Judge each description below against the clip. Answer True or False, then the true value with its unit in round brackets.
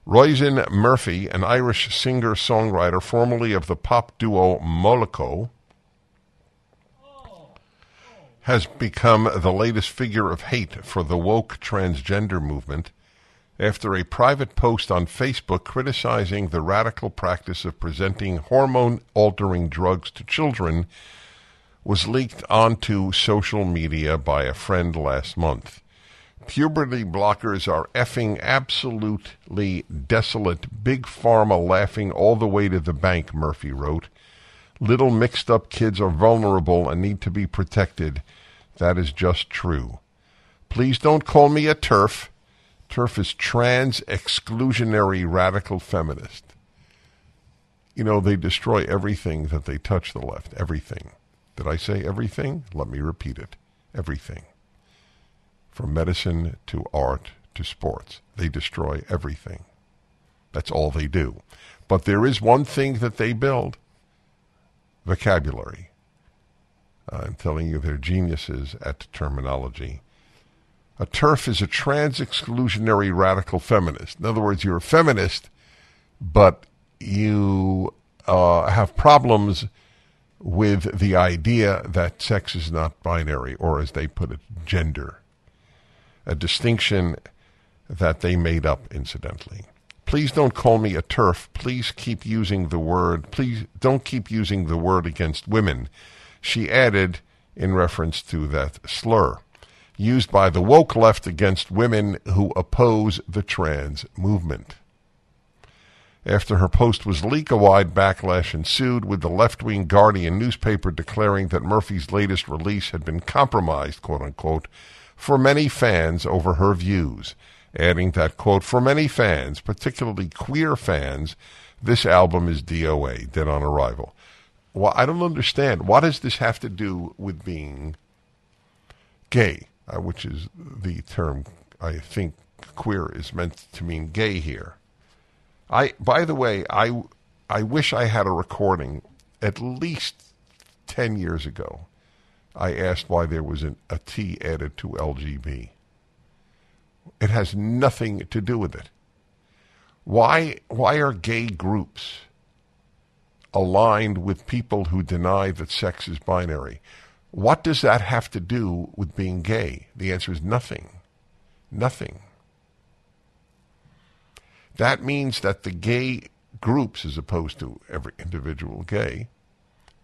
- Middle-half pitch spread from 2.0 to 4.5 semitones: False (5.1 semitones)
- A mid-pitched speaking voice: False (95 Hz)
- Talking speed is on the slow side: True (130 wpm)